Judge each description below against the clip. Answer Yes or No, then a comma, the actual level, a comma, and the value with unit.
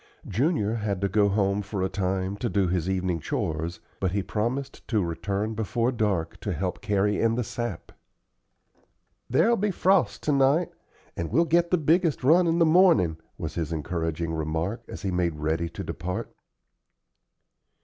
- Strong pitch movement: Yes, wide, 7.1 semitones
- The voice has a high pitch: No, low, 100 Hz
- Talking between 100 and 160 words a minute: No, average, 170 wpm